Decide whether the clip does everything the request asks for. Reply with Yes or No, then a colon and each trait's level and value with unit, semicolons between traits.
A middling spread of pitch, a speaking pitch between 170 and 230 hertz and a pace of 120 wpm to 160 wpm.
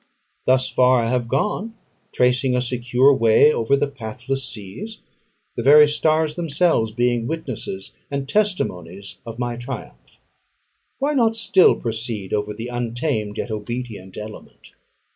No: average, 4.5 semitones; low, 125 Hz; slow, 135 wpm